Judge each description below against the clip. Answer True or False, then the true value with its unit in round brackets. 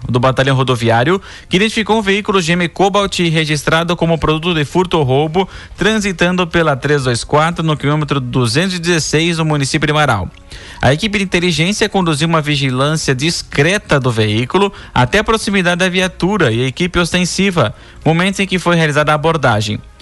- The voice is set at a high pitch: False (160 Hz)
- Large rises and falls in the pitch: False (4.7 semitones)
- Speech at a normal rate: True (155 wpm)